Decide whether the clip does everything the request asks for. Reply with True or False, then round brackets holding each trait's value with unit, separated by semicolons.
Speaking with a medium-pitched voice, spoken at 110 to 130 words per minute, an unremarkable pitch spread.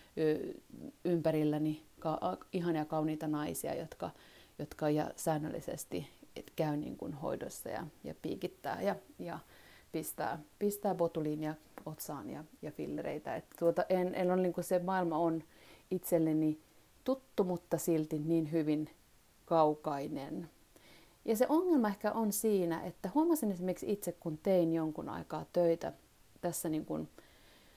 True (170 Hz; 125 wpm; 3.3 semitones)